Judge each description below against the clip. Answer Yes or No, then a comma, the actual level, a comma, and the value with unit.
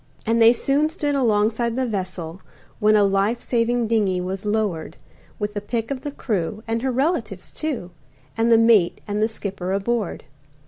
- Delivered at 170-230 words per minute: Yes, average, 175 wpm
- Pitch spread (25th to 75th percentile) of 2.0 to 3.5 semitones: Yes, average, 3.2 semitones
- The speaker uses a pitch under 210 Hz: No, high, 220 Hz